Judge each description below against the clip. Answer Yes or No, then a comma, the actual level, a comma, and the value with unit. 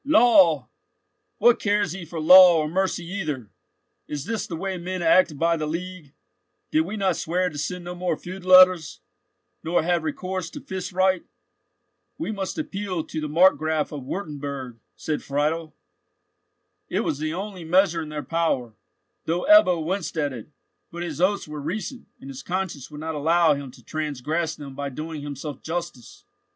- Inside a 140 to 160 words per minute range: No, average, 170 wpm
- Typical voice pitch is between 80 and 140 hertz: No, medium, 165 Hz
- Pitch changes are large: No, average, 3.6 semitones